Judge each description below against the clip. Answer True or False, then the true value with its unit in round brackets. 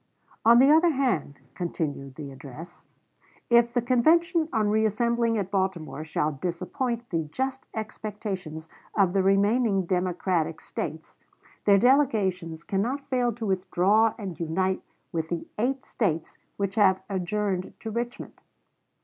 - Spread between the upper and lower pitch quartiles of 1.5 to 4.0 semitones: False (5.2 semitones)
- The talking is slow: True (130 wpm)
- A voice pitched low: False (200 Hz)